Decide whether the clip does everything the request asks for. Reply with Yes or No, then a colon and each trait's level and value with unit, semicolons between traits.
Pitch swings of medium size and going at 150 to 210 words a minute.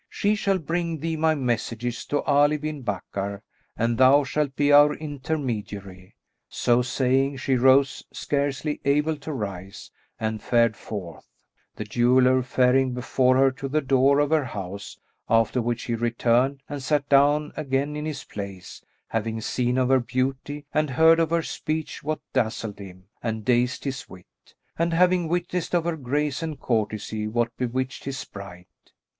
Yes: average, 4.2 semitones; average, 160 wpm